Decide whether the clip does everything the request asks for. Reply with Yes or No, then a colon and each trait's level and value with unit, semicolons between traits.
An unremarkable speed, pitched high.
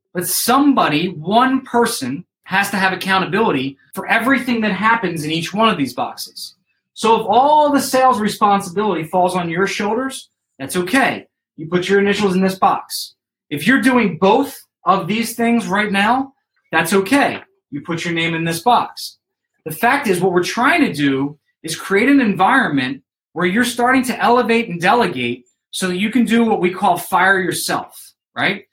Yes: average, 180 wpm; high, 200 Hz